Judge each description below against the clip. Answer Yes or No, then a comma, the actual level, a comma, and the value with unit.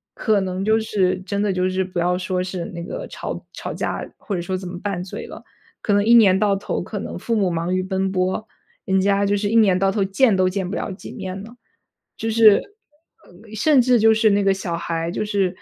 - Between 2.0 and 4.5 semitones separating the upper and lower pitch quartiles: Yes, narrow, 2.4 semitones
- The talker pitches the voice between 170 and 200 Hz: Yes, high, 195 Hz